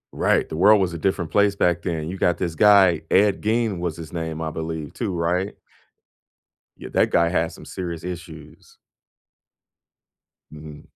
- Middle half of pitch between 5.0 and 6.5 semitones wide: No, average, 2.9 semitones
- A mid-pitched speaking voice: No, very low, 85 Hz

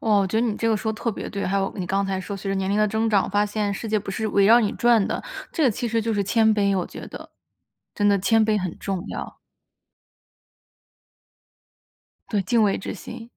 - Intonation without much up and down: Yes, narrow, 2.1 semitones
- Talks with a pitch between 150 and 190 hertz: No, high, 205 Hz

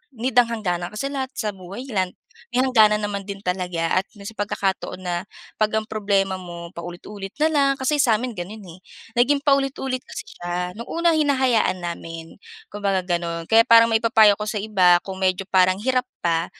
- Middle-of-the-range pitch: No, high, 205 Hz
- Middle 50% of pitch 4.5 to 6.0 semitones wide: Yes, average, 4.9 semitones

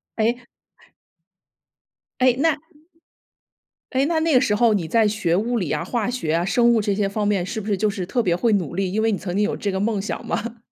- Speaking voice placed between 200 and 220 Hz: Yes, high, 215 Hz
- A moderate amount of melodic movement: Yes, average, 3.5 semitones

